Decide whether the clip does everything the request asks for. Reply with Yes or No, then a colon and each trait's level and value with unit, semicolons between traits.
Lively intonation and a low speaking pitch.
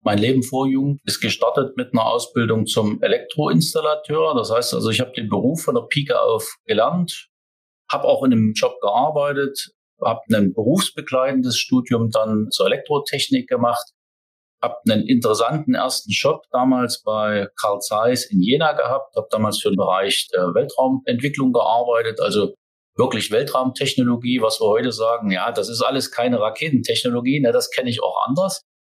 Yes: wide, 6.1 semitones; low, 130 Hz